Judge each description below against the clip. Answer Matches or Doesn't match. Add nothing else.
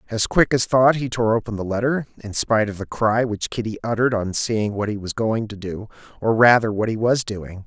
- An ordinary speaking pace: Doesn't match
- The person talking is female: Doesn't match